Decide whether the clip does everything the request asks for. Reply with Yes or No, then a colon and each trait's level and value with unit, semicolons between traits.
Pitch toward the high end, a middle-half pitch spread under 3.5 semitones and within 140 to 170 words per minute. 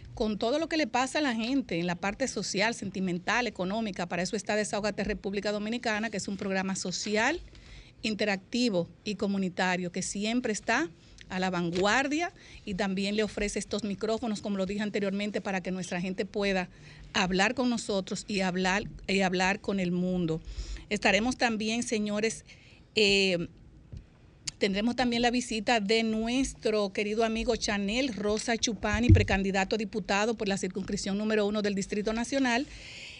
Yes: high, 210 Hz; average, 2.8 semitones; average, 155 wpm